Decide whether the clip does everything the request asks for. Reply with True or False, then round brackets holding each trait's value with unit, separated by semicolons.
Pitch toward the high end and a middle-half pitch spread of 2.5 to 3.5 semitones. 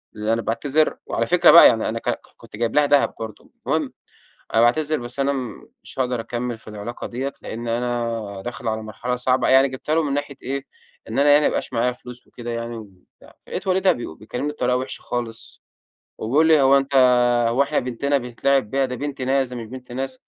False (125 Hz; 2.9 semitones)